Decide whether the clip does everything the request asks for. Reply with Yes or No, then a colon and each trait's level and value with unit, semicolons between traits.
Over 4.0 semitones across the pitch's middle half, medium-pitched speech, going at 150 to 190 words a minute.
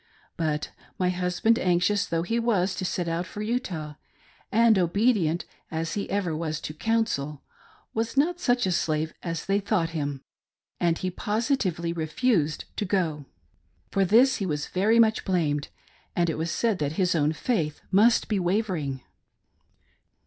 Yes: average, 5.2 semitones; medium, 180 Hz; average, 155 wpm